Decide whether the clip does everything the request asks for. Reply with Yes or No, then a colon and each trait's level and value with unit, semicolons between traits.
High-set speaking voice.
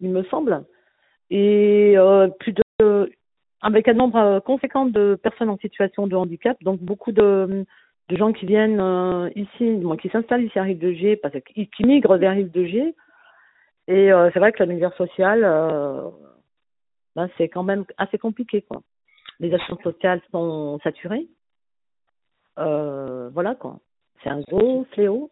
Yes: high, 195 Hz